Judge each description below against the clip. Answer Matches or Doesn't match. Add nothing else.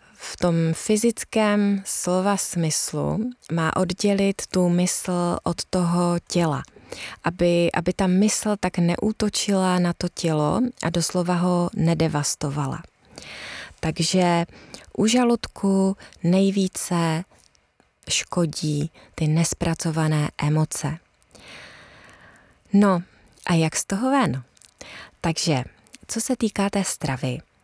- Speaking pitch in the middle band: Matches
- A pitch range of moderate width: Matches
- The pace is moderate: Doesn't match